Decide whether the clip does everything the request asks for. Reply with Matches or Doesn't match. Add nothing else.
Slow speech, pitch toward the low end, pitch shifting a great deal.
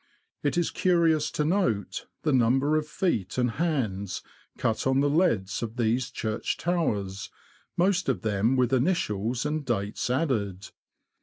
Doesn't match